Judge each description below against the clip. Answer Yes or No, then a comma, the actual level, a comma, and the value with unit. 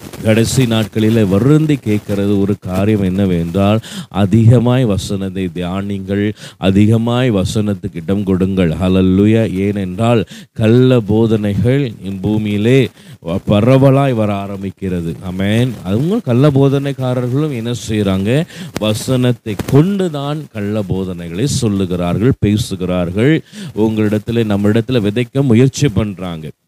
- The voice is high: No, low, 110 Hz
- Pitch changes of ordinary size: Yes, average, 4.4 semitones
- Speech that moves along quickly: No, average, 90 wpm